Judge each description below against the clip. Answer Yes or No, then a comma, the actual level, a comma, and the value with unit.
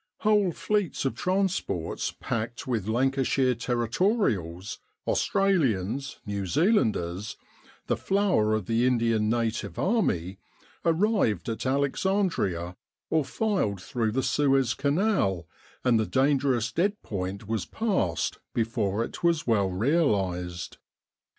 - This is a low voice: Yes, low, 120 Hz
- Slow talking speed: Yes, slow, 110 wpm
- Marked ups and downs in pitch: Yes, wide, 8.6 semitones